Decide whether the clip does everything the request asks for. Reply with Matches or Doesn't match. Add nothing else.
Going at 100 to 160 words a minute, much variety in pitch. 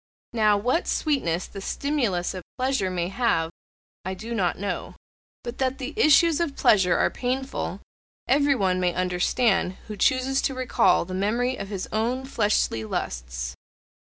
Matches